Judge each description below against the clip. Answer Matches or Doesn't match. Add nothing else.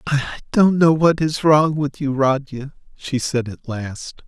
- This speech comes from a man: Matches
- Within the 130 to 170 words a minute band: Doesn't match